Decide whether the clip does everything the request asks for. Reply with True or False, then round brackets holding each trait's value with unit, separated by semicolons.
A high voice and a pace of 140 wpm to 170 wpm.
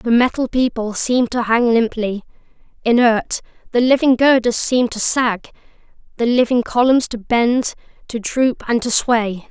True (235 Hz; 150 wpm)